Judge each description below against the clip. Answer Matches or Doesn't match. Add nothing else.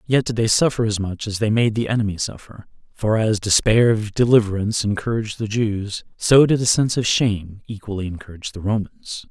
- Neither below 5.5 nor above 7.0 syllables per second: Matches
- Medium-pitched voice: Doesn't match